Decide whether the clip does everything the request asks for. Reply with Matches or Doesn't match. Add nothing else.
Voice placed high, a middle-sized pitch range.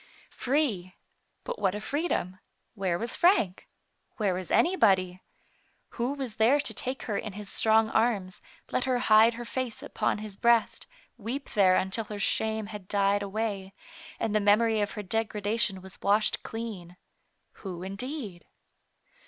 Matches